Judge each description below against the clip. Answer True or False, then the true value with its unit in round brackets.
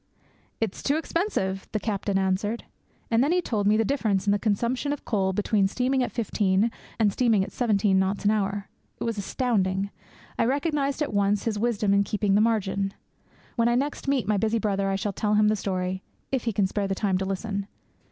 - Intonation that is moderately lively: True (3.1 semitones)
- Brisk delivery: True (210 wpm)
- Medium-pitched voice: False (210 Hz)